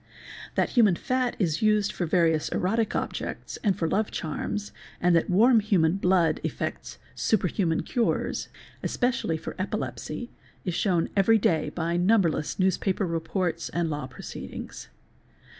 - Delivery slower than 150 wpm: Yes, average, 140 wpm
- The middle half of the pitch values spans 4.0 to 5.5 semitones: Yes, average, 4.3 semitones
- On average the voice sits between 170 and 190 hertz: Yes, medium, 185 Hz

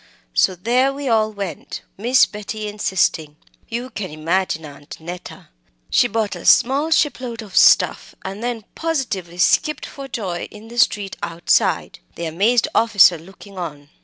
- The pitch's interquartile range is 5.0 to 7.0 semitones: Yes, average, 5.3 semitones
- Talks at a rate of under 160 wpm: Yes, average, 150 wpm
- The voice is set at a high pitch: Yes, high, 210 Hz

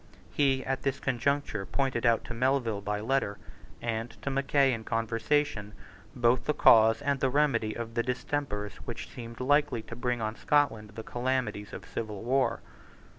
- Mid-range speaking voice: No, low, 120 Hz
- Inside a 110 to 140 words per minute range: No, average, 165 wpm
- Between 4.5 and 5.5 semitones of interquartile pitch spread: No, average, 3.3 semitones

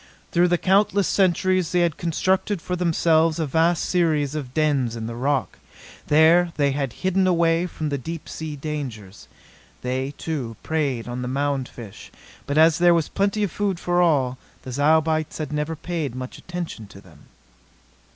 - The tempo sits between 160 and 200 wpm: Yes, average, 170 wpm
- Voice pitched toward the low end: No, medium, 155 Hz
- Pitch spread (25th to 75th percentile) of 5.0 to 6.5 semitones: No, average, 4.3 semitones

